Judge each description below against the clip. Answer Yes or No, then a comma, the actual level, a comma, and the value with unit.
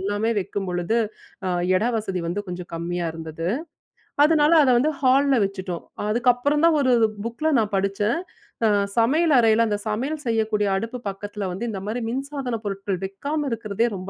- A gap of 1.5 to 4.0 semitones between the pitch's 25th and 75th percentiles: No, average, 4.9 semitones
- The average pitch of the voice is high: Yes, high, 220 Hz